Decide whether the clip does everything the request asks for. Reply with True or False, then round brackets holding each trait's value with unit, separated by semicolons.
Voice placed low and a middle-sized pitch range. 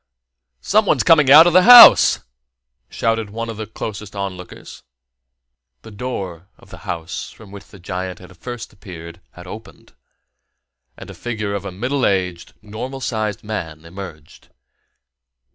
True (105 Hz; 4.1 semitones)